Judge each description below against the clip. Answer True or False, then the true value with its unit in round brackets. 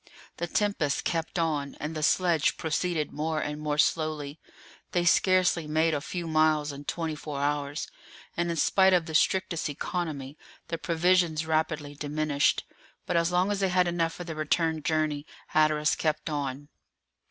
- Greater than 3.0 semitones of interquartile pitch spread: False (2.4 semitones)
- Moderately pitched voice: True (155 Hz)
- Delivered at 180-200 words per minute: False (165 wpm)